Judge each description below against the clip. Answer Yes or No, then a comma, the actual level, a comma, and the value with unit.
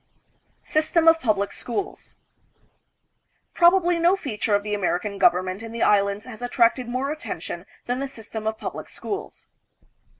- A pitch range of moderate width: No, wide, 7.1 semitones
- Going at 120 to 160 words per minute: Yes, average, 140 wpm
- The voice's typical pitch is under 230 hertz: No, high, 235 Hz